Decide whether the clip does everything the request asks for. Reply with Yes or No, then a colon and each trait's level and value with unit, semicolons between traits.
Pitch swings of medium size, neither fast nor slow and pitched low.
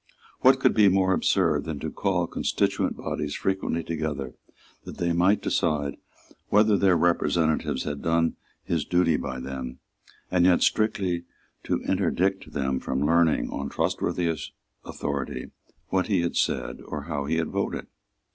Yes: average, 4.1 semitones; average, 145 wpm; very low, 85 Hz